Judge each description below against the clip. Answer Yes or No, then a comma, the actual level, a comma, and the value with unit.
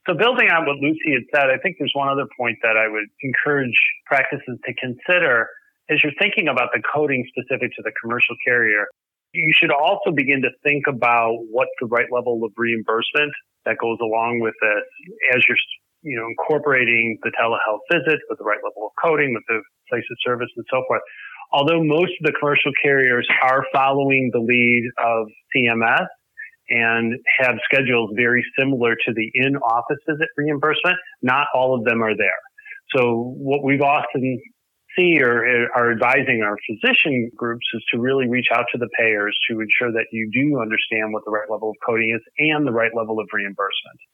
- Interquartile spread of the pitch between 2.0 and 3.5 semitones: No, average, 4.0 semitones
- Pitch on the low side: Yes, low, 125 Hz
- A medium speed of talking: Yes, average, 185 wpm